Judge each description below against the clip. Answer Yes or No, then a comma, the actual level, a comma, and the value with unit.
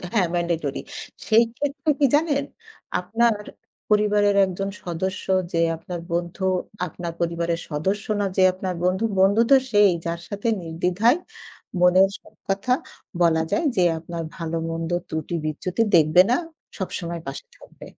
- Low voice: No, medium, 180 Hz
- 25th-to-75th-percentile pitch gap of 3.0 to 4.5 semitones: Yes, average, 3.5 semitones